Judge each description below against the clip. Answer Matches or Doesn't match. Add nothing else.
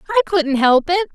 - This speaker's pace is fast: Matches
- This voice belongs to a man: Doesn't match